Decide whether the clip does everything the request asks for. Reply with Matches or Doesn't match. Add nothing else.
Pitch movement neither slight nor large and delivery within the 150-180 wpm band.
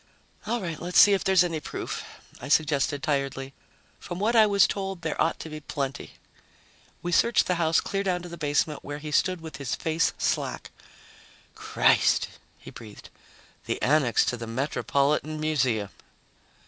Matches